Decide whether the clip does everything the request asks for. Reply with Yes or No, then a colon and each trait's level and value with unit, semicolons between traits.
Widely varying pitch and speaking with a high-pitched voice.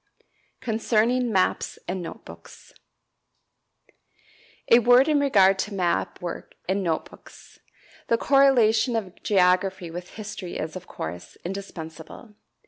No: average, 4.3 semitones; high, 195 Hz